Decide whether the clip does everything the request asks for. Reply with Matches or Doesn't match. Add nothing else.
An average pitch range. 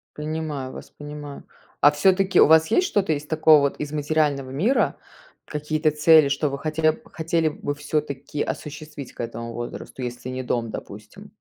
Doesn't match